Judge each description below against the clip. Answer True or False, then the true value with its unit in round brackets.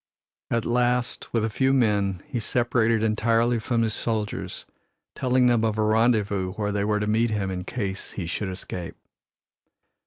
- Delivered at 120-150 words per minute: False (165 wpm)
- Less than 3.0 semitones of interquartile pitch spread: True (2.5 semitones)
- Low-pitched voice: True (110 Hz)